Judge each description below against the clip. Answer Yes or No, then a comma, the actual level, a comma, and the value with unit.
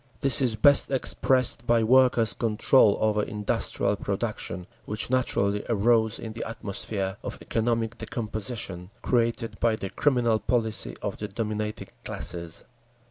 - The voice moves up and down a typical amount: No, narrow, 2.3 semitones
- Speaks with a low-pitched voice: Yes, low, 110 Hz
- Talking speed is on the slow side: Yes, slow, 130 wpm